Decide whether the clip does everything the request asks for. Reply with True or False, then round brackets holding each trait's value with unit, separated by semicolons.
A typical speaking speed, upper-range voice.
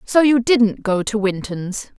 True (180 wpm; 220 Hz)